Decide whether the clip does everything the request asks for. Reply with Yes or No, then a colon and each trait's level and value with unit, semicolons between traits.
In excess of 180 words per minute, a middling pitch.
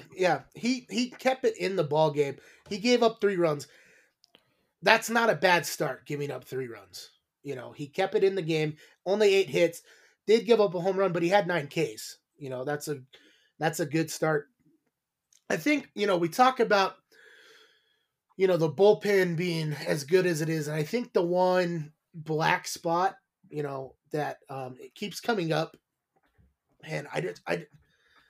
Yes: average, 190 wpm; medium, 175 Hz